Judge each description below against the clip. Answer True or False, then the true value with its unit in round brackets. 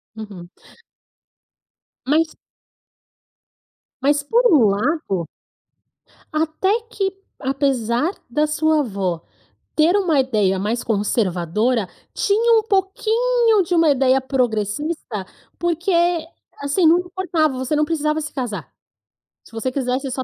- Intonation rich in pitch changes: True (6.5 semitones)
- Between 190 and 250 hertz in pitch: False (285 Hz)